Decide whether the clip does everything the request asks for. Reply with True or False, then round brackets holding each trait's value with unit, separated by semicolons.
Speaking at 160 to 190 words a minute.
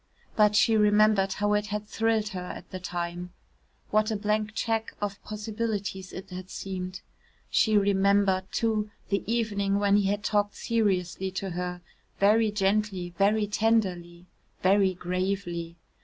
False (140 wpm)